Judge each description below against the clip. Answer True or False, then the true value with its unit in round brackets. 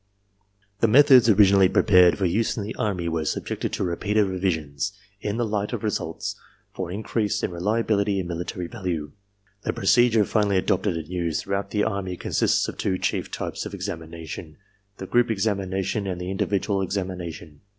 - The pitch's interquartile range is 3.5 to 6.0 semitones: False (2.9 semitones)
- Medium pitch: False (95 Hz)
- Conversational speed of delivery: True (170 wpm)